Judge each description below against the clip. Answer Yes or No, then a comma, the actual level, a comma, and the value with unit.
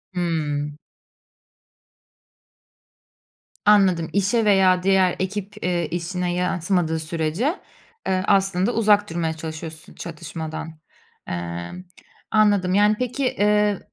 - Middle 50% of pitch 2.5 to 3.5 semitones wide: No, average, 3.9 semitones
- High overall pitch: No, medium, 180 Hz